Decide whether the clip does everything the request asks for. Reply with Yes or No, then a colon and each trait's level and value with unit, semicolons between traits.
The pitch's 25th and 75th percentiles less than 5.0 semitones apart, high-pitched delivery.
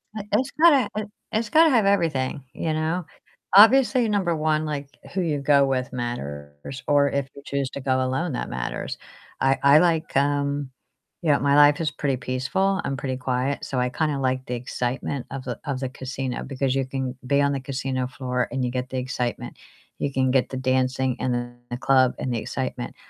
No: average, 2.8 semitones; low, 135 Hz